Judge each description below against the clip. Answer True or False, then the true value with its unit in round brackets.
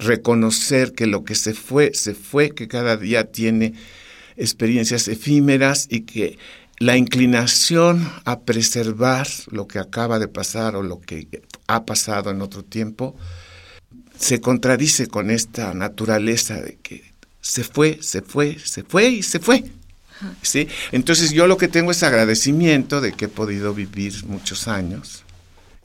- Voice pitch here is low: True (115 Hz)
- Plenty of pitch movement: False (4.5 semitones)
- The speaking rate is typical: True (150 wpm)